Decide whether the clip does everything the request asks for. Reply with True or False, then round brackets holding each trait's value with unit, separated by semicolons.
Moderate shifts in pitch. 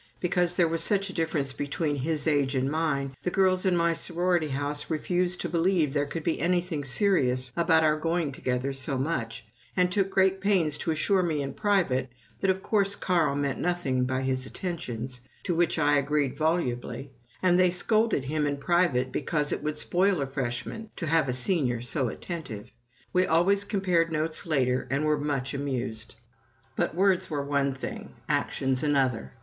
True (4.7 semitones)